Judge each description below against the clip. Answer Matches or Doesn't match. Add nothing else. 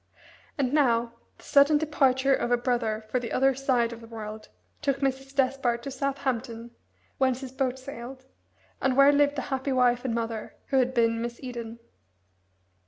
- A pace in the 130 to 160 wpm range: Doesn't match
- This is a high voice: Matches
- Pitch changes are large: Doesn't match